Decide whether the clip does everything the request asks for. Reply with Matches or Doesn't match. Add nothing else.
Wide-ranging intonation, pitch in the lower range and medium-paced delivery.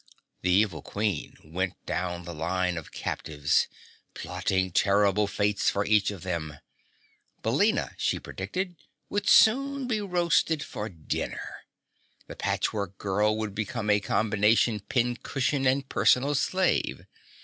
Doesn't match